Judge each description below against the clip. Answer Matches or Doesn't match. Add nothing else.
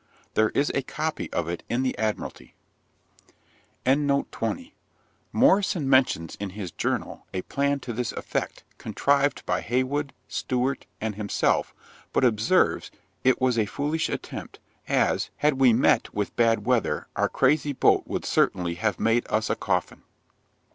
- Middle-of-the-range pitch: Doesn't match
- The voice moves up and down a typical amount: Matches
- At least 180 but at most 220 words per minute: Doesn't match